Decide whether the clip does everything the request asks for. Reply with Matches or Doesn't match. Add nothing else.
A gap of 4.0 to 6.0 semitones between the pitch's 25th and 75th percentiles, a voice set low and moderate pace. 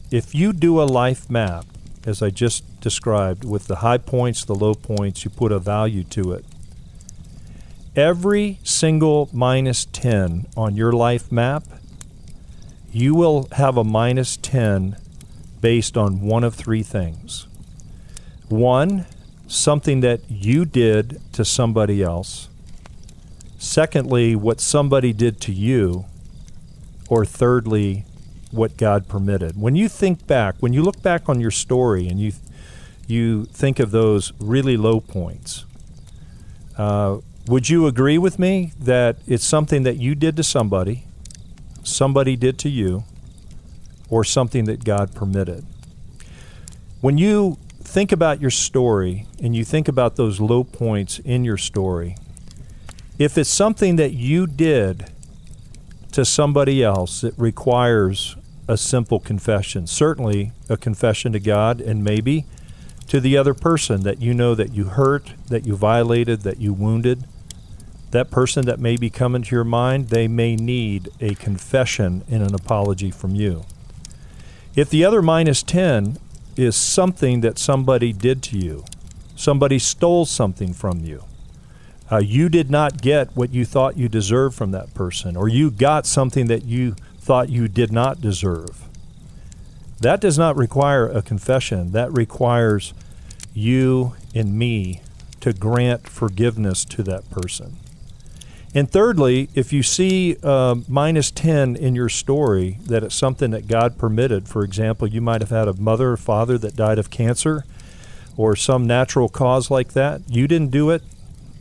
Matches